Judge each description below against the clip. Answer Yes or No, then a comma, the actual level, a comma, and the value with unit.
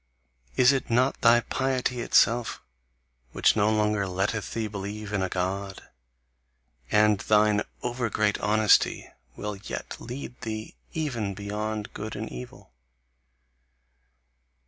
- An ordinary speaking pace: No, slow, 120 wpm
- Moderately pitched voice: No, low, 105 Hz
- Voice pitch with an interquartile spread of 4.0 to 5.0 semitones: No, narrow, 2.6 semitones